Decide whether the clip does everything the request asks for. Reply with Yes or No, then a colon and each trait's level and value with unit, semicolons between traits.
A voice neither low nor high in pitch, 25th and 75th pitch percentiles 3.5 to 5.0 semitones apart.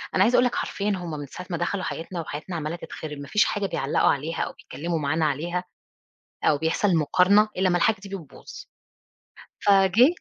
Yes: medium, 175 Hz; average, 4.1 semitones